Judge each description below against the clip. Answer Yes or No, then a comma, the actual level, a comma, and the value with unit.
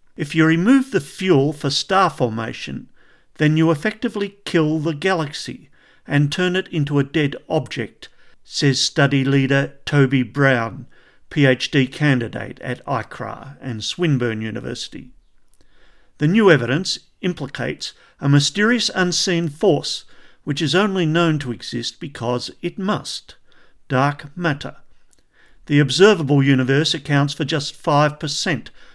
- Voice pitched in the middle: Yes, medium, 145 Hz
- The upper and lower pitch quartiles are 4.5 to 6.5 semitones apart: No, average, 3.7 semitones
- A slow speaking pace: Yes, slow, 120 wpm